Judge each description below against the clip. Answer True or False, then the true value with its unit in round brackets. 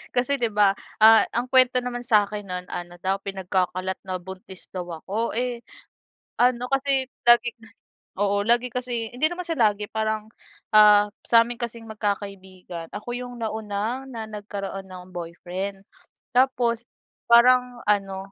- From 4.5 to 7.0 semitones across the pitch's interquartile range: False (3.9 semitones)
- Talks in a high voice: True (215 Hz)